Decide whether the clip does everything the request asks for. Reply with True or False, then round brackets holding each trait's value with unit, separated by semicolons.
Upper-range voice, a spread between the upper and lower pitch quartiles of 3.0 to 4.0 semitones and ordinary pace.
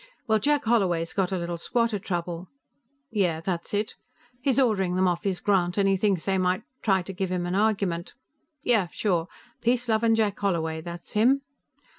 True (195 Hz; 3.7 semitones; 180 wpm)